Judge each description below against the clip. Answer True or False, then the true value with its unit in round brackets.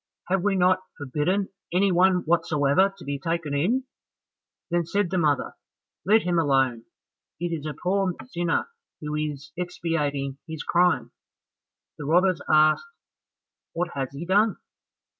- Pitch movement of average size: True (3.9 semitones)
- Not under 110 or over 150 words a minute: True (140 wpm)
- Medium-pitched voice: True (170 Hz)